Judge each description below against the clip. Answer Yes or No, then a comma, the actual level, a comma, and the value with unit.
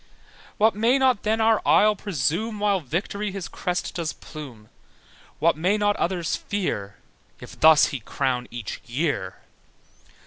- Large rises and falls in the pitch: Yes, wide, 6.8 semitones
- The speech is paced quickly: No, average, 140 wpm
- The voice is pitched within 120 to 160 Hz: No, medium, 180 Hz